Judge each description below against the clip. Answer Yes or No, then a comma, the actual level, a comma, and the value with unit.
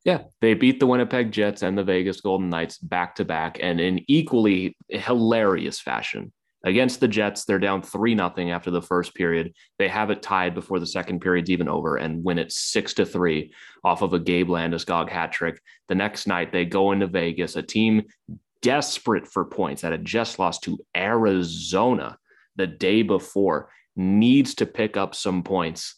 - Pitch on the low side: Yes, very low, 95 Hz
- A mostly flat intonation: No, average, 3.6 semitones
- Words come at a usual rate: Yes, average, 185 wpm